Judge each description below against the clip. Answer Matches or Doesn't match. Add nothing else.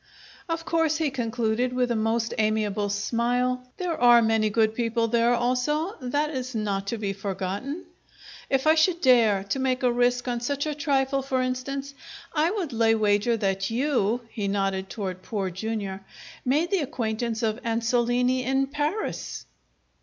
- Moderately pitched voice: Doesn't match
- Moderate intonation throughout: Matches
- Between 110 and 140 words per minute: Doesn't match